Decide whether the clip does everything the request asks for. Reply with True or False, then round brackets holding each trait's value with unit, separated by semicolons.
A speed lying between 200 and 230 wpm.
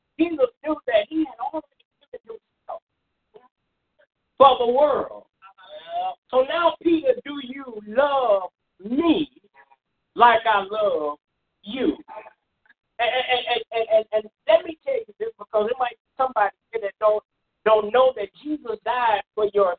False (140 wpm)